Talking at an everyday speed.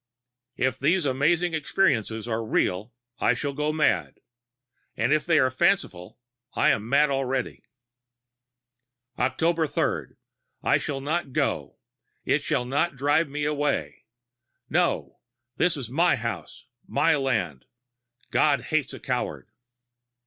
No: slow, 120 wpm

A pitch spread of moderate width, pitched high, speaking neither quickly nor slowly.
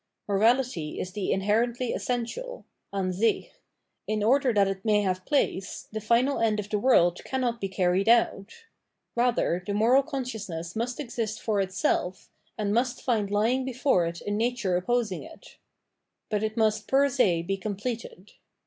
Yes: average, 4.0 semitones; high, 215 Hz; average, 160 wpm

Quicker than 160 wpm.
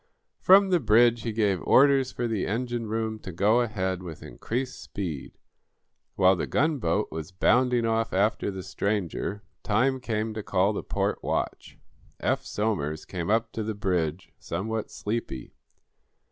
No: average, 150 wpm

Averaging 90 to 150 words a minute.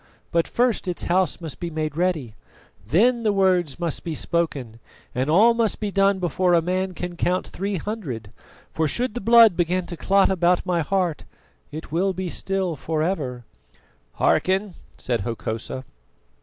No: average, 165 wpm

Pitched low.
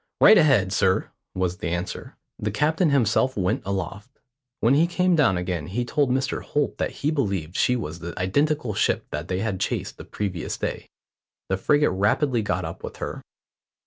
Yes: low, 105 Hz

